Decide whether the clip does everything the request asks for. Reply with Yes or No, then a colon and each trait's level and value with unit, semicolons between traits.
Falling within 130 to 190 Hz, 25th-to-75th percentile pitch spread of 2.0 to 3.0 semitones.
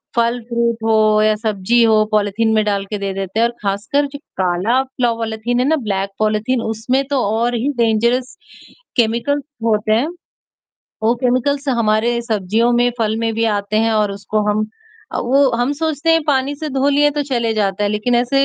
No: high, 230 Hz; average, 2.7 semitones